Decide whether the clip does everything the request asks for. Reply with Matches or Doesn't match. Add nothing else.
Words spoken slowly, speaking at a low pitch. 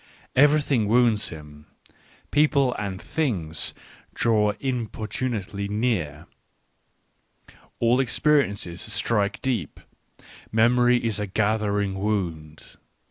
Matches